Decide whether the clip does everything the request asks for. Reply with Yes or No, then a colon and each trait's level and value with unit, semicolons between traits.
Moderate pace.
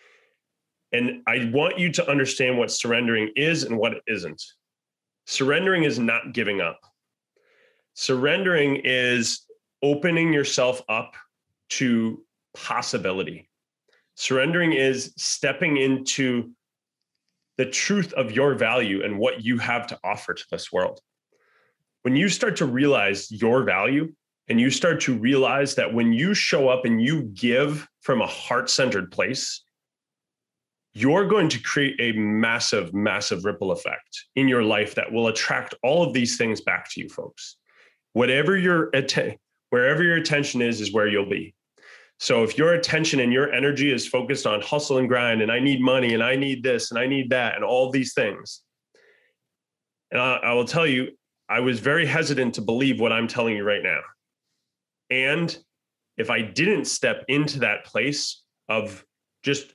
Yes: average, 160 wpm